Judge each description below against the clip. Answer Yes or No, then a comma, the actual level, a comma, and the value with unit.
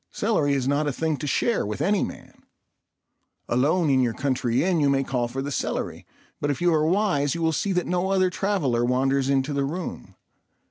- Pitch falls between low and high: Yes, medium, 145 Hz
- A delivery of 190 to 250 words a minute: Yes, fast, 205 wpm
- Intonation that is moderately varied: Yes, average, 4.8 semitones